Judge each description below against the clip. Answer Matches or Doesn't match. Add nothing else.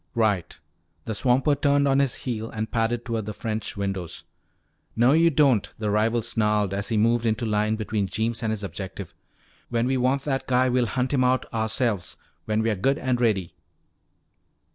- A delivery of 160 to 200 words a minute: Matches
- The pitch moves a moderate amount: Matches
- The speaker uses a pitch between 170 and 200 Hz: Doesn't match